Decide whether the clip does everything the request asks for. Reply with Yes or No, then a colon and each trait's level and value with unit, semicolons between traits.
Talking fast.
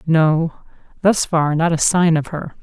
No: average, 185 wpm